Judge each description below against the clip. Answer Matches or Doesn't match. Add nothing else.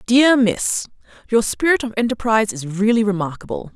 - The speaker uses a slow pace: Matches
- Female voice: Matches